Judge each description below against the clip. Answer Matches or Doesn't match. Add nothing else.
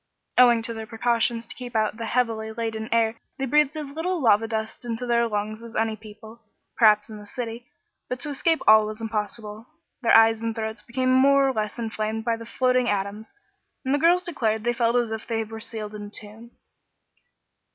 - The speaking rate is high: Matches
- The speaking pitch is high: Matches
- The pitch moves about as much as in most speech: Doesn't match